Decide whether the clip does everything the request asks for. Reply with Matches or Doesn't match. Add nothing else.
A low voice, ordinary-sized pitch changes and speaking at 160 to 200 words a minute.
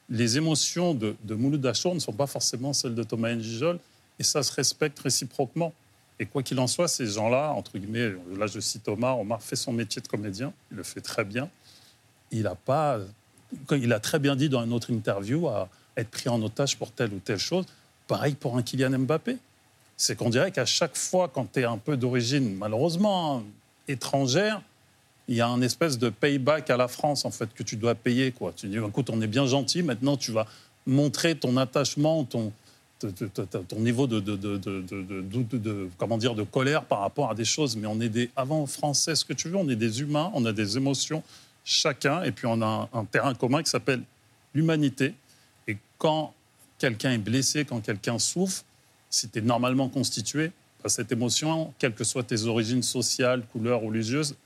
Matches